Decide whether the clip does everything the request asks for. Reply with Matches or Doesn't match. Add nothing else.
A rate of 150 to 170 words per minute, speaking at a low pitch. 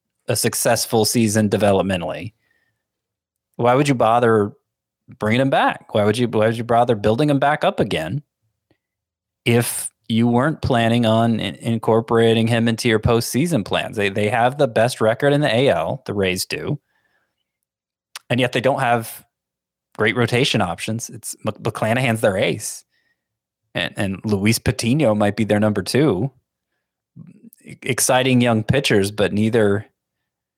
Doesn't match